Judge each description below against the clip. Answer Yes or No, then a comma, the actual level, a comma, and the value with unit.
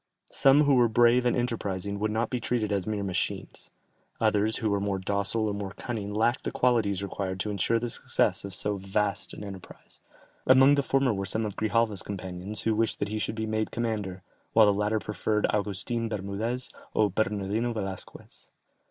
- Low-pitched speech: Yes, low, 105 Hz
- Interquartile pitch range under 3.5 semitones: Yes, narrow, 2.5 semitones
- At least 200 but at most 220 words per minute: No, average, 185 wpm